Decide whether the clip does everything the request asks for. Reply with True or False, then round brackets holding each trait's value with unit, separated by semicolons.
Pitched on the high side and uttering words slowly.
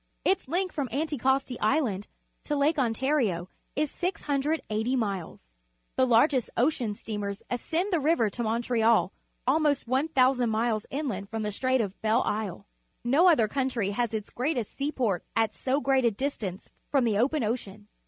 False (245 Hz; 160 wpm)